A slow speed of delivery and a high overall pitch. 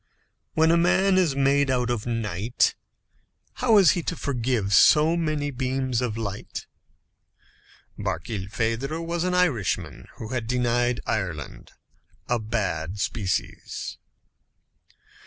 No: slow, 115 wpm; low, 125 Hz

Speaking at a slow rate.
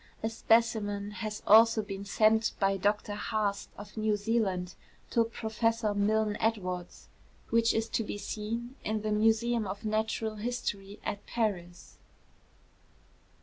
Yes: slow, 130 wpm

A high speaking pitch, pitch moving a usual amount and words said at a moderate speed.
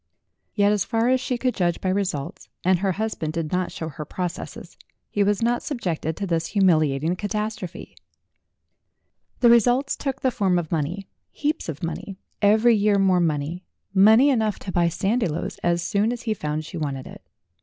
Yes: high, 195 Hz; average, 4.7 semitones; average, 175 wpm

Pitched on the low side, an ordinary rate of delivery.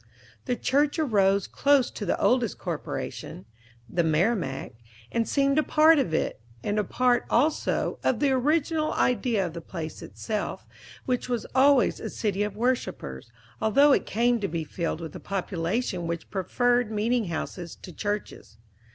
No: high, 220 Hz; average, 160 wpm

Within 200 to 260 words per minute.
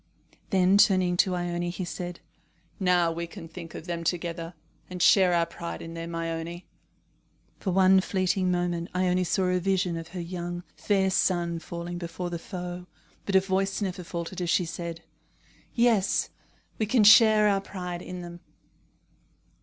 No: average, 160 wpm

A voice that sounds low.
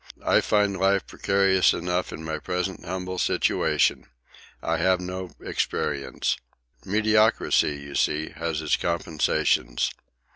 Yes: very low, 90 Hz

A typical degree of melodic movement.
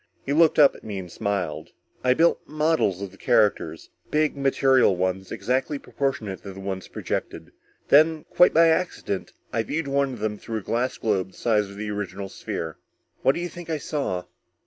No: wide, 7.0 semitones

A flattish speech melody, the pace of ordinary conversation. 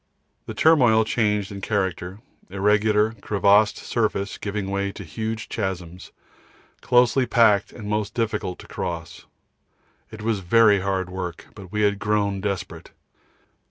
No: narrow, 2.2 semitones; slow, 130 wpm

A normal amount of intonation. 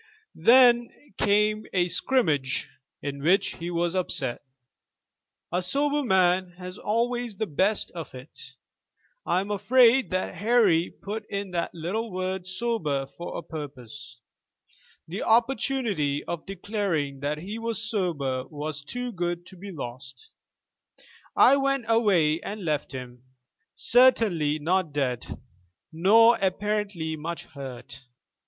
No: wide, 6.3 semitones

